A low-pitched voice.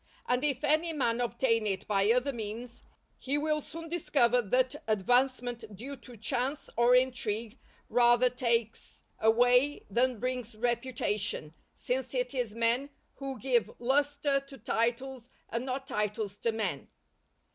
No: high, 245 Hz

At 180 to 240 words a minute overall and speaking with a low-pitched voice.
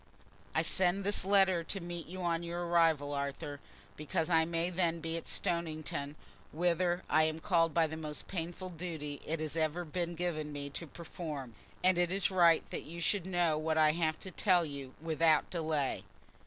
No: average, 185 wpm; medium, 165 Hz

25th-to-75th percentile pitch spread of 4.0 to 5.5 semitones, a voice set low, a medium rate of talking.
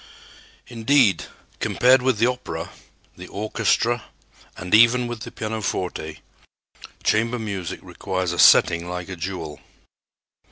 No: average, 4.8 semitones; low, 110 Hz; slow, 115 wpm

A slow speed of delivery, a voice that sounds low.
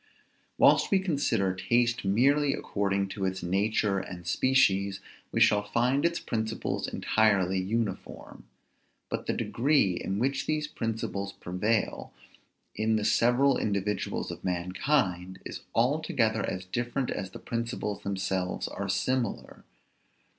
Yes: slow, 125 wpm; low, 110 Hz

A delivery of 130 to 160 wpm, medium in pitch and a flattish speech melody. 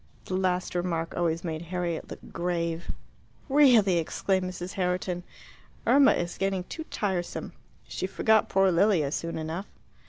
Yes: slow, 135 wpm; medium, 180 Hz; narrow, 2.3 semitones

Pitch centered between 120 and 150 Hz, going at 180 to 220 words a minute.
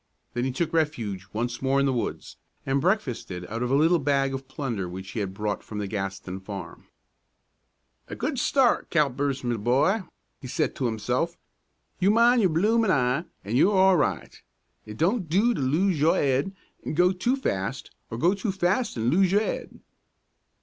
Yes: medium, 140 Hz; average, 185 wpm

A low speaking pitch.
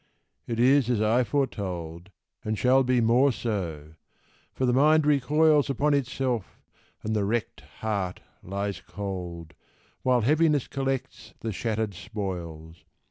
Yes: low, 115 Hz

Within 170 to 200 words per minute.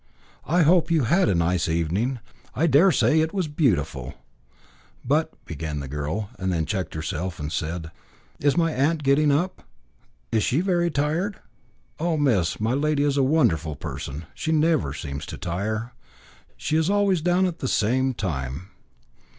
No: average, 160 wpm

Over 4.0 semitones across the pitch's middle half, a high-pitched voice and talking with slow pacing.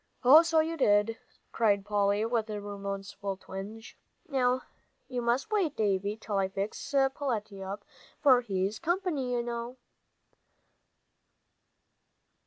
Yes: average, 4.7 semitones; high, 225 Hz; slow, 120 wpm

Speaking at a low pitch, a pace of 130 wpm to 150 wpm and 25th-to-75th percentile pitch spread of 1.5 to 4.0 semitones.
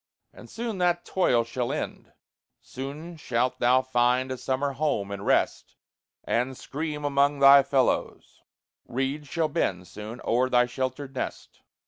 Yes: low, 130 Hz; average, 140 wpm; average, 2.9 semitones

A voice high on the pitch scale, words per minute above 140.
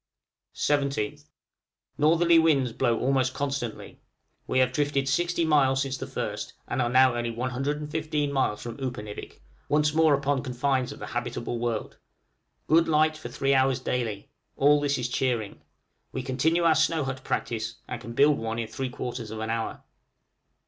No: low, 135 Hz; average, 160 wpm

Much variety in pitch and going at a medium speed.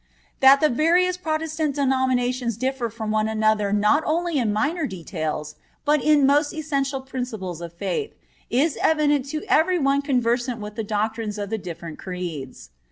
Yes: wide, 5.9 semitones; average, 160 wpm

